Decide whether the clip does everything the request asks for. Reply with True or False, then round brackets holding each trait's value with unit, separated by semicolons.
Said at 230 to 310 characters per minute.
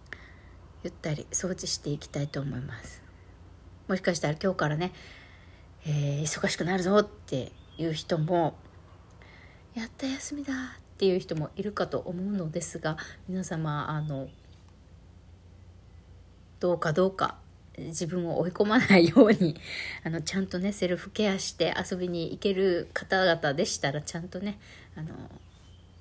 True (280 characters per minute)